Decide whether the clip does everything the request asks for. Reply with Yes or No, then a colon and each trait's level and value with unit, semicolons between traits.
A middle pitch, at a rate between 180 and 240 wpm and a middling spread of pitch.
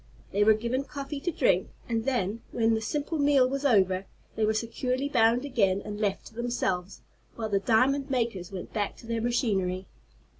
No: high, 230 Hz; average, 185 wpm; average, 4.1 semitones